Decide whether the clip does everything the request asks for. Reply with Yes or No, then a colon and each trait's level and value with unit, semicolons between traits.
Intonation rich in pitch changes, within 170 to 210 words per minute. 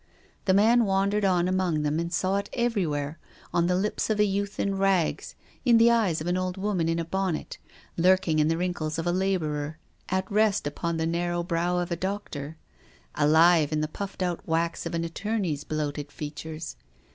No: average, 3.4 semitones; average, 190 wpm